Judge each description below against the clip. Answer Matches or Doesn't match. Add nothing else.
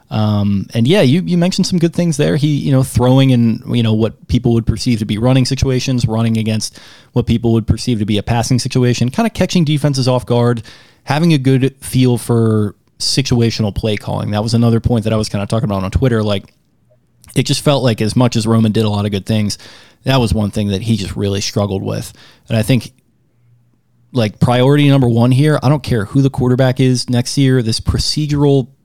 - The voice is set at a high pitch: Doesn't match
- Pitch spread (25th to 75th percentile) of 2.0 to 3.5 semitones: Matches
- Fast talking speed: Matches